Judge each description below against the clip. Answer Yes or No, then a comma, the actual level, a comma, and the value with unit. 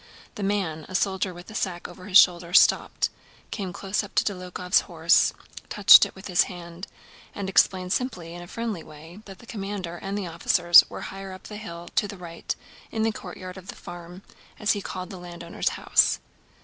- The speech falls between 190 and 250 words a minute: Yes, average, 200 wpm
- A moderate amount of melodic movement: No, narrow, 2.3 semitones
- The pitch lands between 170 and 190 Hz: Yes, medium, 185 Hz